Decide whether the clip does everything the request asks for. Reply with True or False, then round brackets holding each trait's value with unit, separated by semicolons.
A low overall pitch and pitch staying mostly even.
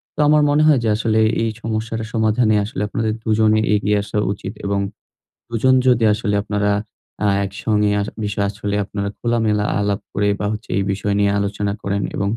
True (105 Hz; 1.7 semitones)